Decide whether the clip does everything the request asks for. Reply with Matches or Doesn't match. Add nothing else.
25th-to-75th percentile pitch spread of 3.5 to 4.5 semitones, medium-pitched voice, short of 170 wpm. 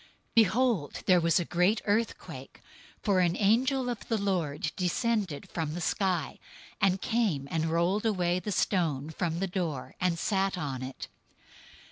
Matches